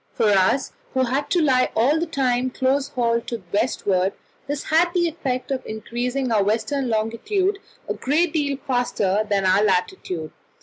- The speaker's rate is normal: Yes, average, 170 wpm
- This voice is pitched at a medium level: No, very high, 255 Hz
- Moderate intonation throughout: Yes, average, 4.8 semitones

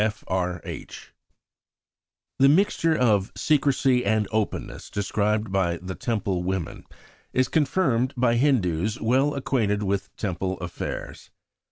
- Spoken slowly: Yes, slow, 120 wpm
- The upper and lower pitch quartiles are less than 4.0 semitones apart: No, wide, 5.4 semitones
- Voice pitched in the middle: No, low, 110 Hz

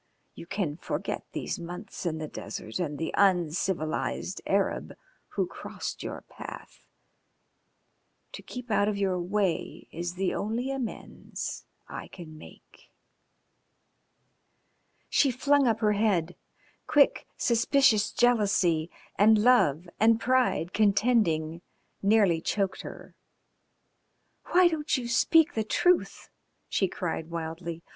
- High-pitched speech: Yes, high, 200 Hz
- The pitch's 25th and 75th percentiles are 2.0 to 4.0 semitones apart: No, wide, 5.6 semitones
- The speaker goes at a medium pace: No, slow, 115 wpm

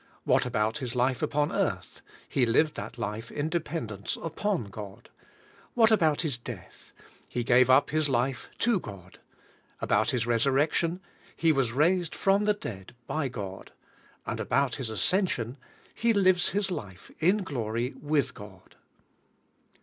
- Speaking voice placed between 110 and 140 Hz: Yes, low, 135 Hz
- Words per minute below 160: Yes, average, 145 wpm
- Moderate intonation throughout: No, wide, 6.5 semitones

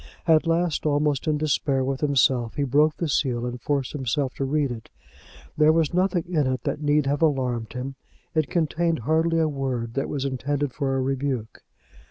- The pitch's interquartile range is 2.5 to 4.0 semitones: Yes, average, 3.0 semitones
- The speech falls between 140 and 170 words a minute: No, average, 190 wpm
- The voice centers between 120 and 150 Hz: Yes, medium, 140 Hz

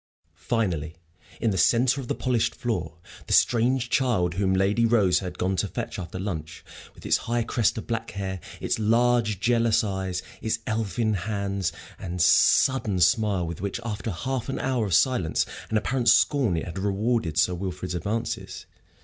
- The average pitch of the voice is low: Yes, low, 105 Hz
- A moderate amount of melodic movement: Yes, average, 4.3 semitones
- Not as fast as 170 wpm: No, average, 175 wpm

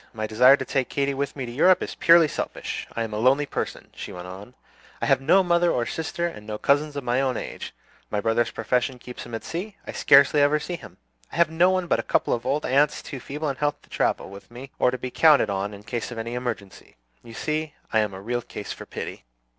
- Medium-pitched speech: No, low, 130 Hz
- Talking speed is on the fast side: Yes, fast, 250 wpm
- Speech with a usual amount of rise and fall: Yes, average, 4.8 semitones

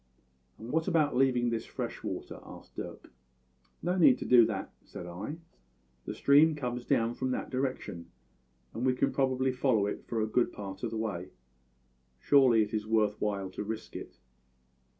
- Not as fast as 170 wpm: No, average, 175 wpm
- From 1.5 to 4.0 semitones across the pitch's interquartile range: Yes, average, 3.7 semitones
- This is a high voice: No, low, 120 Hz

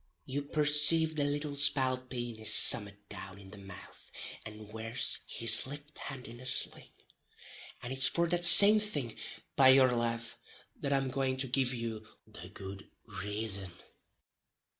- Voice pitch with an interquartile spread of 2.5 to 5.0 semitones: Yes, average, 4.6 semitones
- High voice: No, low, 130 Hz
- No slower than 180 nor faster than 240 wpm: No, average, 150 wpm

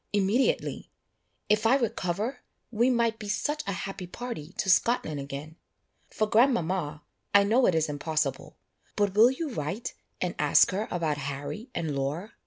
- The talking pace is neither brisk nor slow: Yes, average, 155 wpm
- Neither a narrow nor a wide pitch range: No, wide, 6.6 semitones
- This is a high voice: Yes, high, 200 Hz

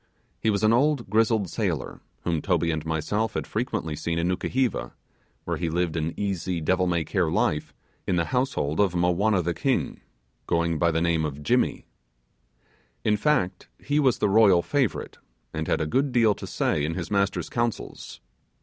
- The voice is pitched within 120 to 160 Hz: No, very low, 90 Hz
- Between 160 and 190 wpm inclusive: Yes, average, 175 wpm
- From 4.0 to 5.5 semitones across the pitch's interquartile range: Yes, average, 5.1 semitones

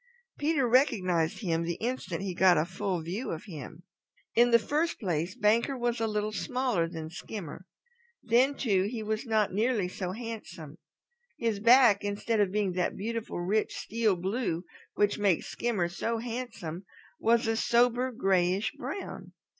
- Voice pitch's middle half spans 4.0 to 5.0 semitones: Yes, average, 4.5 semitones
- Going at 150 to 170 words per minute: Yes, average, 155 wpm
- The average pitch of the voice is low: No, high, 210 Hz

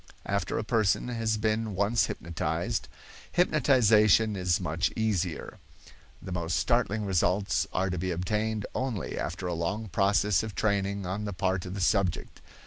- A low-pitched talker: Yes, low, 100 Hz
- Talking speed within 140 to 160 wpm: Yes, average, 150 wpm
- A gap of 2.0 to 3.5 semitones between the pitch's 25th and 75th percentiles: Yes, average, 3.2 semitones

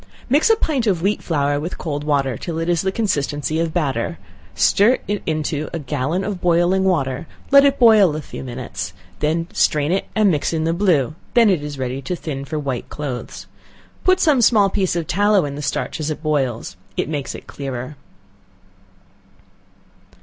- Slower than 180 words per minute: No, average, 190 wpm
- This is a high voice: No, medium, 160 Hz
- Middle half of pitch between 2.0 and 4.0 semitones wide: No, average, 5.1 semitones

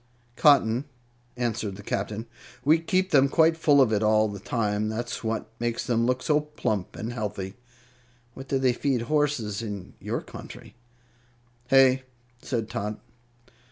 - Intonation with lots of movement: No, average, 4.2 semitones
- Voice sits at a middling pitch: No, low, 120 Hz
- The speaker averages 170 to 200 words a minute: No, average, 155 wpm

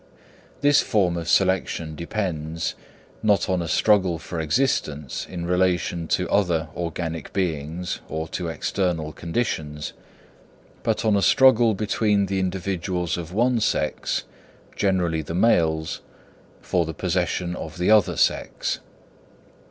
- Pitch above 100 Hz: No, very low, 90 Hz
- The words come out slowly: Yes, slow, 125 wpm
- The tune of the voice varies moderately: Yes, average, 3.2 semitones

